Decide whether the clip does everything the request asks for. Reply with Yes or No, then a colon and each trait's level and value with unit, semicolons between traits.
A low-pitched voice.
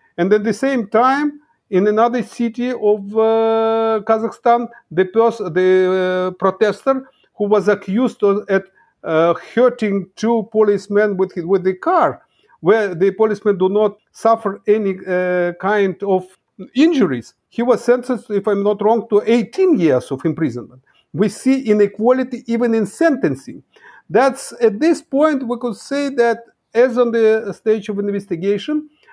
No: high, 220 Hz